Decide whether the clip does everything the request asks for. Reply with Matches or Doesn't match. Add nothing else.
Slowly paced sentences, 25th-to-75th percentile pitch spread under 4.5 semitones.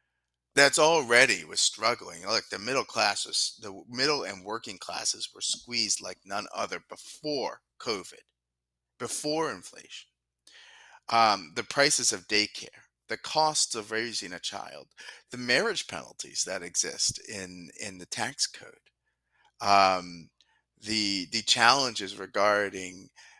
Doesn't match